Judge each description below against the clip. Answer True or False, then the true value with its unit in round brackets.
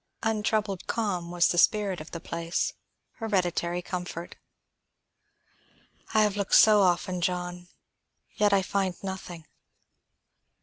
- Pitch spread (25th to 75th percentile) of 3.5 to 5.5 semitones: False (2.8 semitones)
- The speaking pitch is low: False (185 Hz)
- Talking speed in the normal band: False (115 wpm)